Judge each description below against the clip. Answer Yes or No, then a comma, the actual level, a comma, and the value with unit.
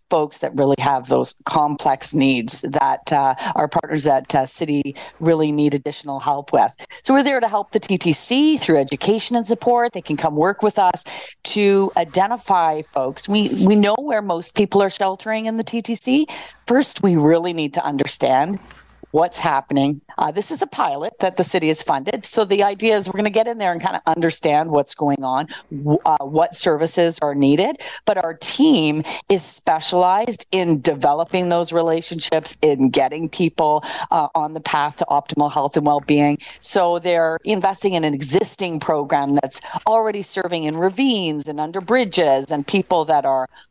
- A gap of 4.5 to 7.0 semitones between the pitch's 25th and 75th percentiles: Yes, average, 5.2 semitones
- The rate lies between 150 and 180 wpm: Yes, average, 175 wpm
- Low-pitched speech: No, medium, 165 Hz